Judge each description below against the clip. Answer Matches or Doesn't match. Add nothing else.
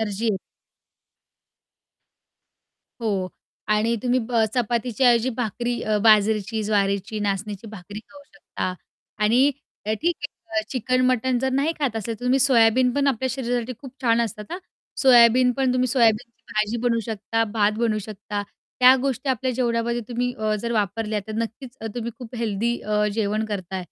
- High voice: Matches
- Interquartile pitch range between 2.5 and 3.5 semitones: Matches